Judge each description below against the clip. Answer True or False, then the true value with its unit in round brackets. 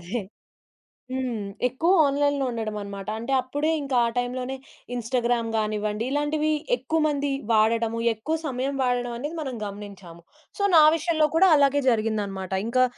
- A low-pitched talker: False (245 Hz)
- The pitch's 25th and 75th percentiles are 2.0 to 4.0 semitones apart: False (4.7 semitones)